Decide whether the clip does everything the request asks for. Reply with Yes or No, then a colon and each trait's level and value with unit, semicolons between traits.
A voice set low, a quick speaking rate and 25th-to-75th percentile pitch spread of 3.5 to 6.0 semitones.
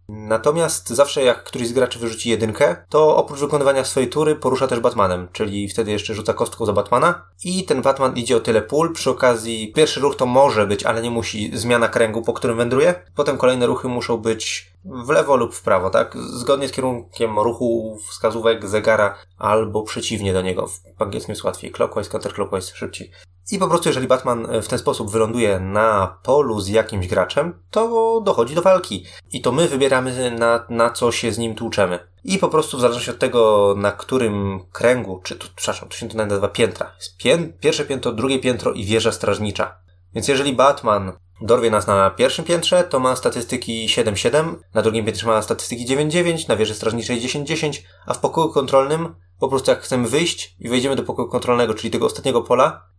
Yes: low, 115 Hz; fast, 190 wpm; average, 3.9 semitones